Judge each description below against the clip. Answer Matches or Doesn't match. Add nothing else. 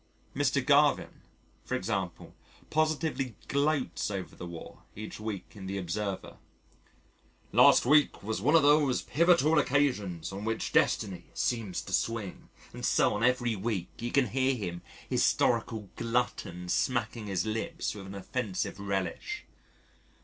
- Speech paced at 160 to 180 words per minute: Doesn't match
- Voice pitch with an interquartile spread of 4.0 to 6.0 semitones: Matches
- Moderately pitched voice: Doesn't match